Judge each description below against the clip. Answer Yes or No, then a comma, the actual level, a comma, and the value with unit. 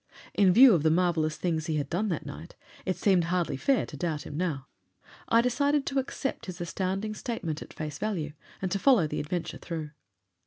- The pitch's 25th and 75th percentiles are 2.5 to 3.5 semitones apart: No, average, 5.3 semitones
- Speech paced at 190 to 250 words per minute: Yes, average, 200 wpm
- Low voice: No, medium, 175 Hz